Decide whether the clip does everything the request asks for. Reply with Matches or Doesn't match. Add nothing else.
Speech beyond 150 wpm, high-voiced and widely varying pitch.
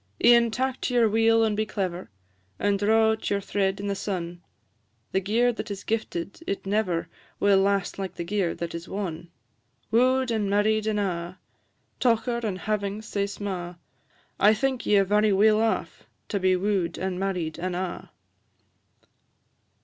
Doesn't match